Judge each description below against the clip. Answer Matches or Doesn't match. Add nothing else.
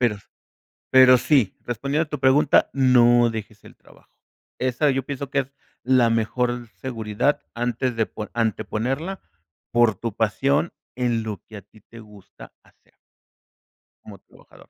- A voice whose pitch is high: Doesn't match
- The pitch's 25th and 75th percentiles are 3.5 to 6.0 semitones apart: Doesn't match